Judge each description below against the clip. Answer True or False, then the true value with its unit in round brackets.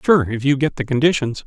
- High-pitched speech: False (135 Hz)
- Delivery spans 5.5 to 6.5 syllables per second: True (5.8 syllables/s)